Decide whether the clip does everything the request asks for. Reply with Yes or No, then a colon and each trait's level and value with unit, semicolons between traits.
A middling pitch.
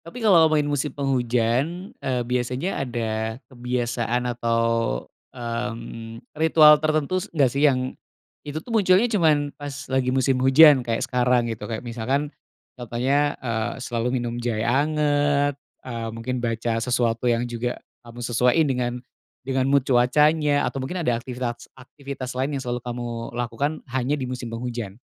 No: low, 125 Hz